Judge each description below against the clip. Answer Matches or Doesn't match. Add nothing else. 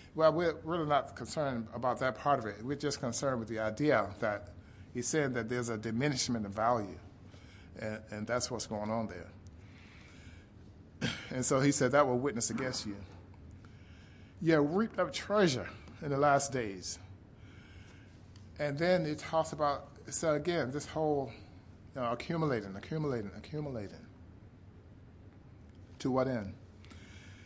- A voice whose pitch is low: Matches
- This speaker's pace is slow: Doesn't match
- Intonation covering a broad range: Matches